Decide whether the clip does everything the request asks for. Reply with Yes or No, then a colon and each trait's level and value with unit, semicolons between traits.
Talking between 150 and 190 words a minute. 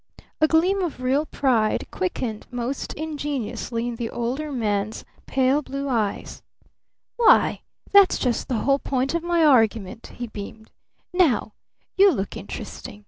No: average, 140 wpm